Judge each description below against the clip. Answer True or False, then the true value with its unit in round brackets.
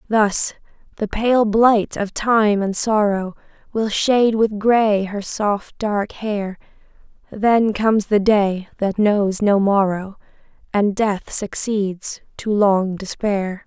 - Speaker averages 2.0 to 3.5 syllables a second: True (3.3 syllables/s)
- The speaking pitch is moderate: False (205 Hz)